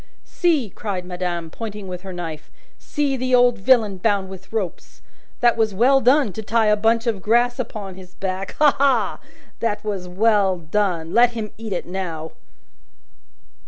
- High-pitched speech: Yes, high, 210 Hz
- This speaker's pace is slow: No, average, 165 wpm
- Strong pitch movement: No, average, 4.1 semitones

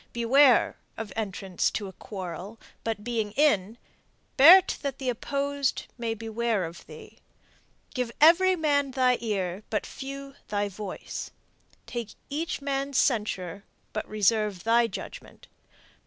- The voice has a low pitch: No, high, 230 Hz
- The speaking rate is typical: No, slow, 130 wpm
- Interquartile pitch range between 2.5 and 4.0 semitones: No, average, 5.0 semitones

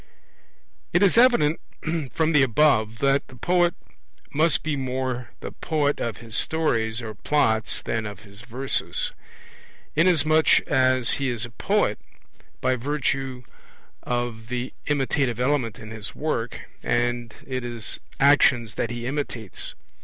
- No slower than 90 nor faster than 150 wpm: Yes, slow, 135 wpm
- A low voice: Yes, low, 130 Hz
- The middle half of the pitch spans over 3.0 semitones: Yes, average, 4.1 semitones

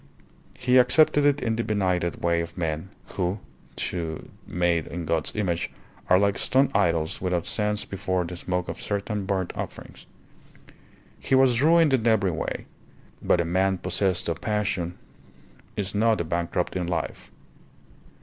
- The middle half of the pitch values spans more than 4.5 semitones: No, average, 3.8 semitones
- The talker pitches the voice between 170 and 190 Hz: No, very low, 95 Hz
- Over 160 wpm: No, average, 150 wpm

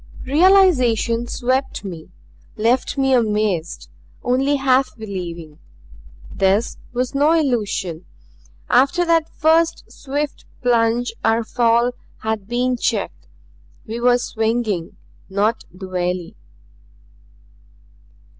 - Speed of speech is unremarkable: No, slow, 95 wpm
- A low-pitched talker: No, high, 235 Hz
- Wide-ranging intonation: No, average, 4.5 semitones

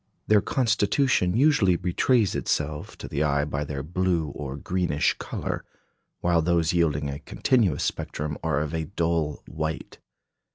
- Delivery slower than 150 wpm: Yes, average, 140 wpm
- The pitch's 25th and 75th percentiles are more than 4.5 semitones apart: No, average, 3.9 semitones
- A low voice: Yes, very low, 80 Hz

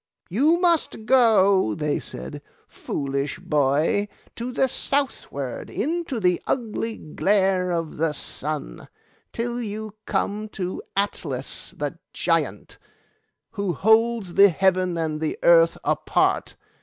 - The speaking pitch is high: Yes, high, 195 Hz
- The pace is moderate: No, slow, 115 wpm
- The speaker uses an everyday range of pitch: No, wide, 5.7 semitones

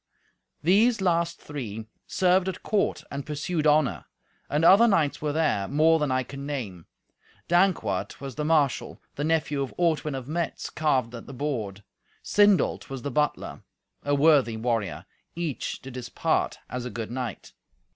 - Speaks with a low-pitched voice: No, medium, 145 Hz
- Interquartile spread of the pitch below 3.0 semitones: No, average, 4.5 semitones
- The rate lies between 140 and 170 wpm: Yes, average, 160 wpm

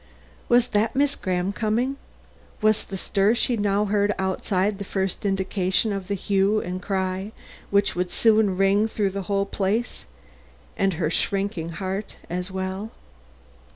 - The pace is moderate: Yes, average, 150 wpm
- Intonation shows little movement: Yes, narrow, 2.0 semitones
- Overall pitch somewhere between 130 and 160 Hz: No, high, 195 Hz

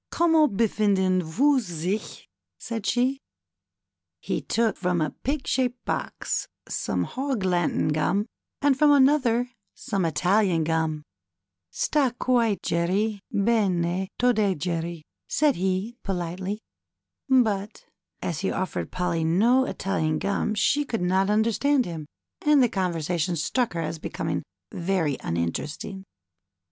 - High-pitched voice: Yes, high, 195 Hz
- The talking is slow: Yes, slow, 125 wpm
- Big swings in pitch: Yes, wide, 6.0 semitones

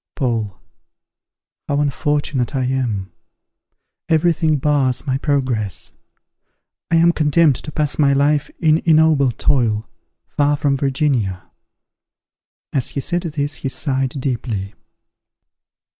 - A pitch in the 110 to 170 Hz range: Yes, medium, 140 Hz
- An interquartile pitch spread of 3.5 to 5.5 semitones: No, average, 2.9 semitones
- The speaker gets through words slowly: Yes, slow, 115 wpm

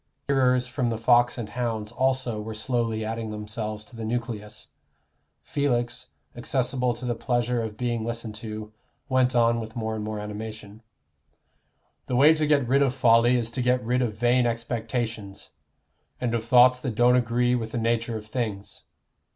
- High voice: No, low, 120 Hz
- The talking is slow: No, average, 170 wpm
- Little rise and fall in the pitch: Yes, narrow, 2.0 semitones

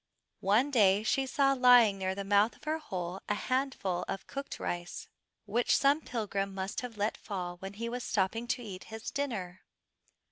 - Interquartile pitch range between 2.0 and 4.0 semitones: No, average, 4.6 semitones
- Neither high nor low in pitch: No, high, 215 Hz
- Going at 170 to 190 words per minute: Yes, average, 180 wpm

